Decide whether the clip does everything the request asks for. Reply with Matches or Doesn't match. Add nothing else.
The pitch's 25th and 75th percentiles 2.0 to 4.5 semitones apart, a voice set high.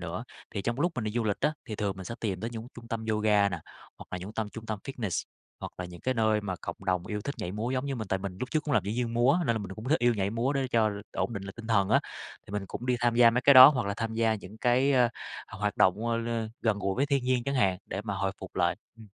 Doesn't match